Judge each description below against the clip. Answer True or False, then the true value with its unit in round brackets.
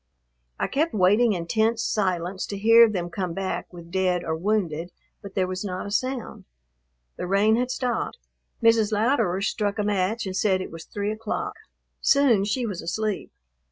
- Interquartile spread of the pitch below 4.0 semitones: True (3.4 semitones)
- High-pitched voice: True (205 Hz)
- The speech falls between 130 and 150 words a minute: False (175 wpm)